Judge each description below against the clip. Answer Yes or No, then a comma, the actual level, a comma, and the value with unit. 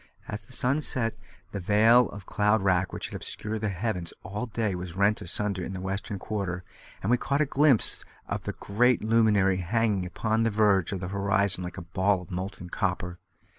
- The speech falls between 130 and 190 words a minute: No, average, 200 wpm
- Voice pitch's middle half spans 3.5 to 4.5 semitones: No, average, 3.1 semitones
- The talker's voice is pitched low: Yes, low, 100 Hz